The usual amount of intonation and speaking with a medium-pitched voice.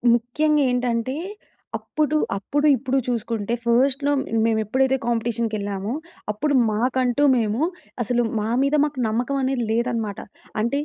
No: average, 3.1 semitones; high, 240 Hz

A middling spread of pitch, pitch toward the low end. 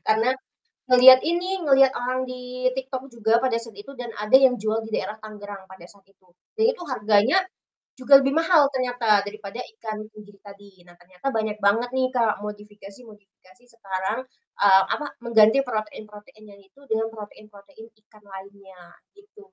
No: average, 3.9 semitones; high, 220 Hz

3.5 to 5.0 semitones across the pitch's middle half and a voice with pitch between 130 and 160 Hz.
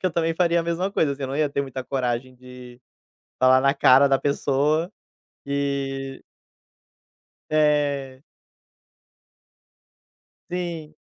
No: narrow, 2.6 semitones; medium, 140 Hz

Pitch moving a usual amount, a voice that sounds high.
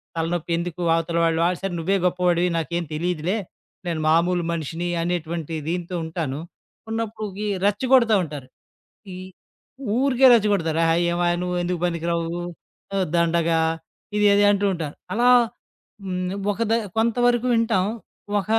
No: average, 3.5 semitones; medium, 175 Hz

